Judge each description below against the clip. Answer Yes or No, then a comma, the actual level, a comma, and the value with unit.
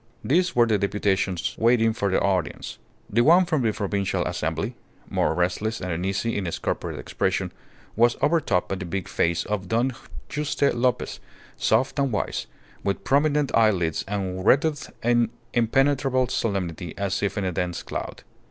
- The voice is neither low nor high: No, low, 110 Hz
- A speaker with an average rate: Yes, average, 160 wpm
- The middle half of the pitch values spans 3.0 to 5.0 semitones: No, wide, 5.5 semitones